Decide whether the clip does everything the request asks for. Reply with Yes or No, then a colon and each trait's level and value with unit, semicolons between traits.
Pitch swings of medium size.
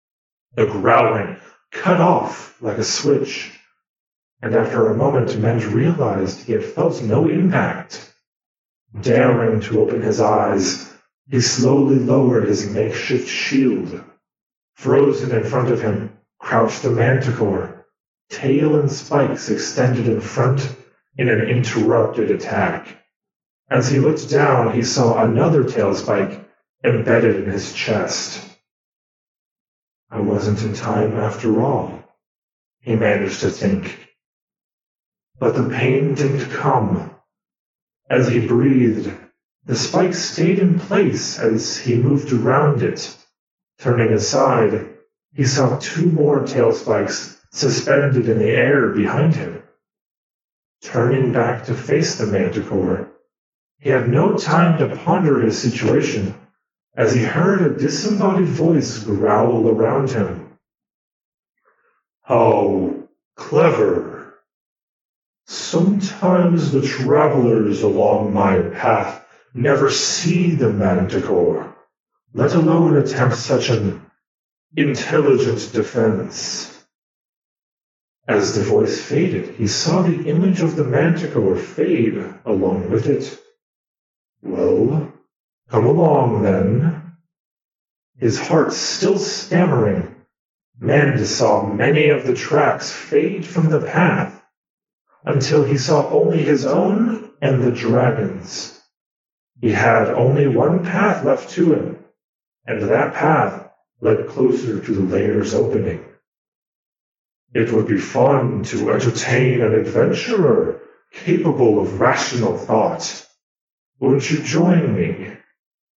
No: wide, 5.8 semitones